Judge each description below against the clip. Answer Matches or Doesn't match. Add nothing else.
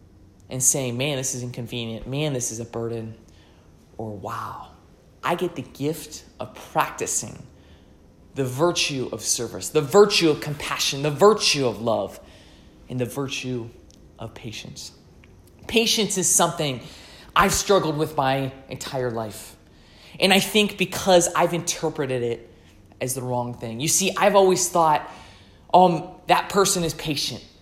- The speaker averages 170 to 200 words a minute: Doesn't match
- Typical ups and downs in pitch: Doesn't match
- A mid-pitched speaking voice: Doesn't match